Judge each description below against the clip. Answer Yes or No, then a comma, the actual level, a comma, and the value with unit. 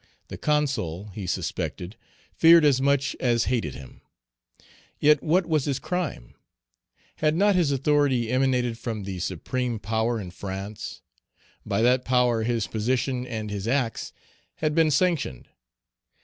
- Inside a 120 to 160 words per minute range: Yes, slow, 135 wpm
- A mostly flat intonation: No, average, 5.1 semitones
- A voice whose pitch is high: No, low, 125 Hz